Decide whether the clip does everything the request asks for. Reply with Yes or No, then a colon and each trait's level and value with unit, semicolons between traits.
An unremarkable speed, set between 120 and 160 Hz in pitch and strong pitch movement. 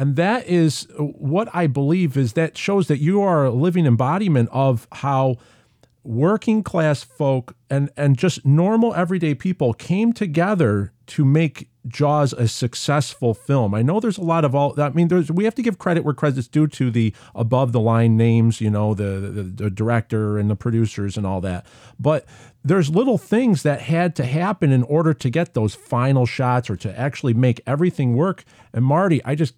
Yes: average, 195 wpm; medium, 140 Hz; wide, 5.7 semitones